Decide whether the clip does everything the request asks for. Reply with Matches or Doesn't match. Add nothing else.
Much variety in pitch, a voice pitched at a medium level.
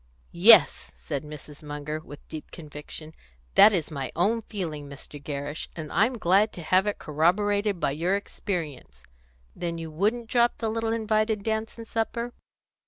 Matches